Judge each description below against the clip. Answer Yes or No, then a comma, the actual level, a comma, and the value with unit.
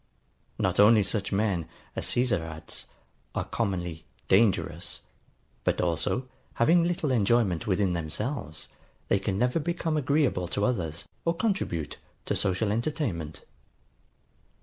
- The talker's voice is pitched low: Yes, low, 100 Hz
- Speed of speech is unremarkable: No, slow, 120 wpm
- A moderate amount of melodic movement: No, wide, 6.4 semitones